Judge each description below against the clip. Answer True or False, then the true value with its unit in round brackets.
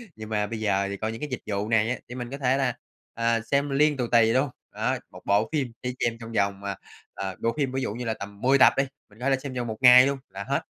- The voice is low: True (115 Hz)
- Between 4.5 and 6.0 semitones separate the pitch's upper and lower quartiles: False (3.6 semitones)